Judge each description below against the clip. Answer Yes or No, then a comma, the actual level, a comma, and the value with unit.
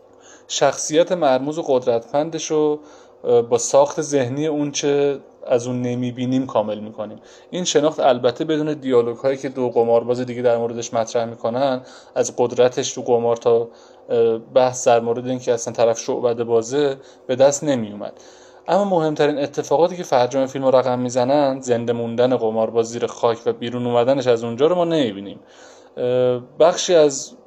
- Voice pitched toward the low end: Yes, low, 130 Hz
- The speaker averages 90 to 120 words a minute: No, average, 150 wpm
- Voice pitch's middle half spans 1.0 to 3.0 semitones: No, average, 3.7 semitones